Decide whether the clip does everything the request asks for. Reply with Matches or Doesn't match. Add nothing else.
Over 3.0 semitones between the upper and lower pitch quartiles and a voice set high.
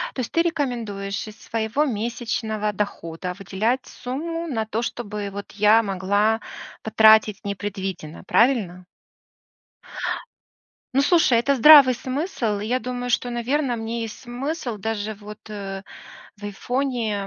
Matches